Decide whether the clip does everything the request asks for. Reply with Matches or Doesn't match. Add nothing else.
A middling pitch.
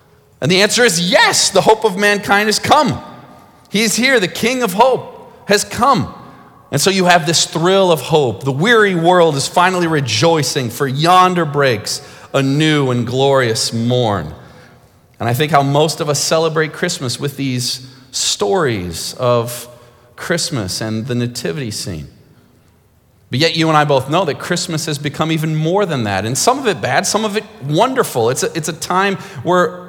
Matches